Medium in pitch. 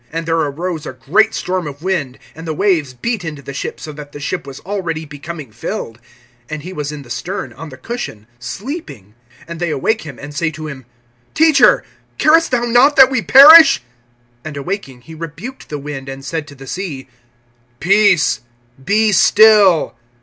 Yes: medium, 160 Hz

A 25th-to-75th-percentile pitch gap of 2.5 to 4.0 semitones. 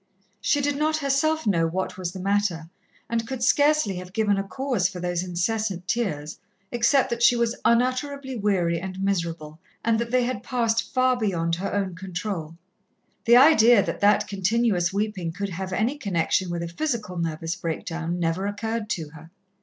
No: average, 5.3 semitones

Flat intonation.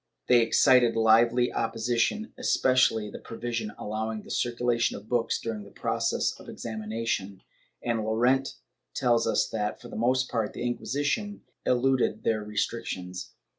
Yes: narrow, 2.1 semitones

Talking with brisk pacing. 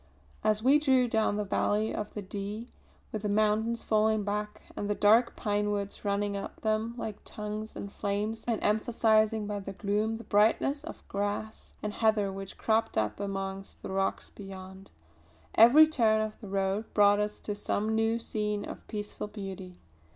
No: average, 170 wpm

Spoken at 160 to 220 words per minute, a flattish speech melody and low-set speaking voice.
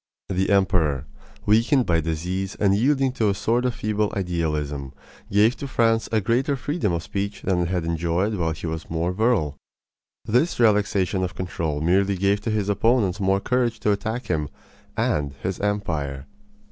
No: average, 170 wpm; average, 4.8 semitones; low, 100 Hz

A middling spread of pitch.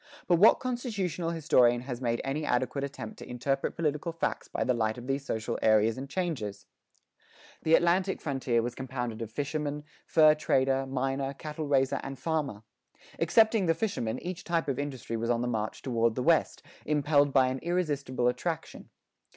Yes: average, 4.8 semitones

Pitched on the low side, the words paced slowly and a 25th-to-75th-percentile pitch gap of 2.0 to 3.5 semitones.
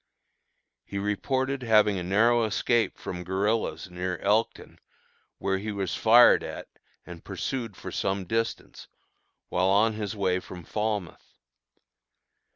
Yes: low, 105 Hz; slow, 125 wpm; average, 3.0 semitones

